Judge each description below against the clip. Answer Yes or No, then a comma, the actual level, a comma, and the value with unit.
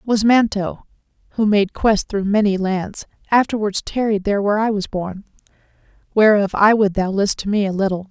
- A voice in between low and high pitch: No, high, 205 Hz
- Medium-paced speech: Yes, average, 180 wpm